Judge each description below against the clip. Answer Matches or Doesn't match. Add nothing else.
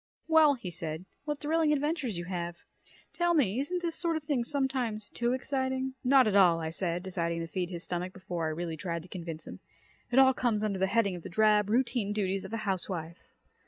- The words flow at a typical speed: Doesn't match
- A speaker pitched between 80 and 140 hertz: Doesn't match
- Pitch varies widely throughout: Matches